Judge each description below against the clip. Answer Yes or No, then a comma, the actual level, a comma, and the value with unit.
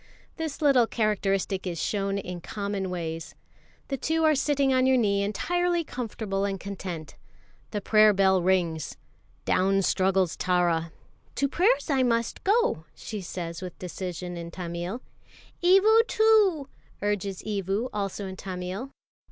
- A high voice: Yes, high, 200 Hz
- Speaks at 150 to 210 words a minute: No, slow, 135 wpm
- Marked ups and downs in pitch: Yes, wide, 6.3 semitones